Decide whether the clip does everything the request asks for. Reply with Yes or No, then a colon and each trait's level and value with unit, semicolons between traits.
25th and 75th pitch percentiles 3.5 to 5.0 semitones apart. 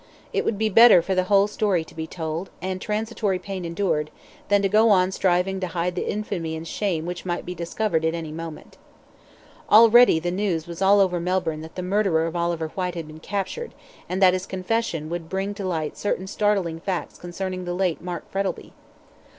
No: average, 2.9 semitones